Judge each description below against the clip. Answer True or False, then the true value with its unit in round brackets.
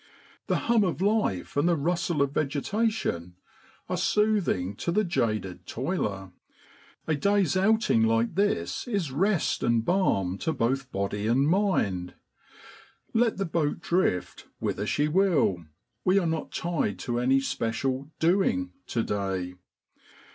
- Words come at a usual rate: True (150 wpm)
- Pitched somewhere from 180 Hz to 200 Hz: False (150 Hz)